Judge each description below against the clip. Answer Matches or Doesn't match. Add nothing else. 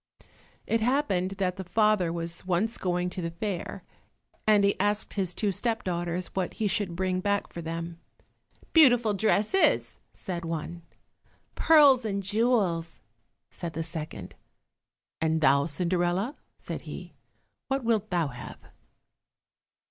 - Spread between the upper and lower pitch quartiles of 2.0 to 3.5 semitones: Doesn't match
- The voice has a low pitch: Doesn't match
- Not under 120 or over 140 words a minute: Matches